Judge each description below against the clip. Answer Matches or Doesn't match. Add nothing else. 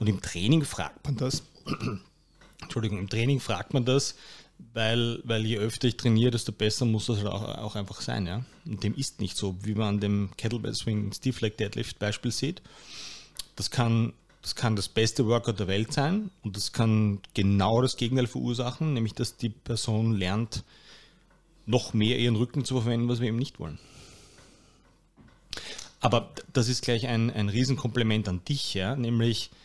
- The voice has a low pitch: Matches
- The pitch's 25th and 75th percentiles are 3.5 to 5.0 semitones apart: Doesn't match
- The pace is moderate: Matches